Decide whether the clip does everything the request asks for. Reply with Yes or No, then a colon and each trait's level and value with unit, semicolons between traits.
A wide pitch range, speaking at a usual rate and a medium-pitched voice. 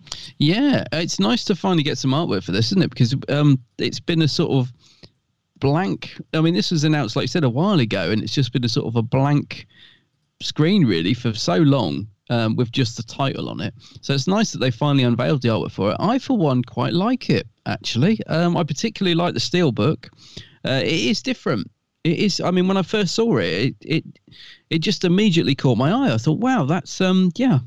No: wide, 6.0 semitones; fast, 225 wpm; medium, 150 Hz